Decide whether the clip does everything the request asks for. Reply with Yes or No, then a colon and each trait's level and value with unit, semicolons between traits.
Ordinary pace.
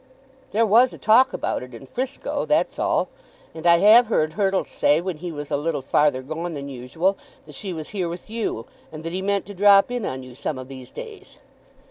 No: fast, 220 wpm